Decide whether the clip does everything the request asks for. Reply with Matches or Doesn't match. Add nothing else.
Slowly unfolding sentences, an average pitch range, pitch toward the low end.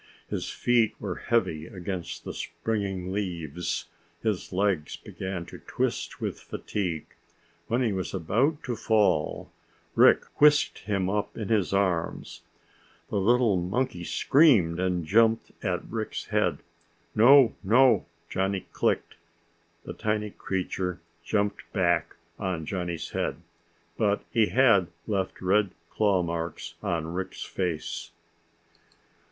Matches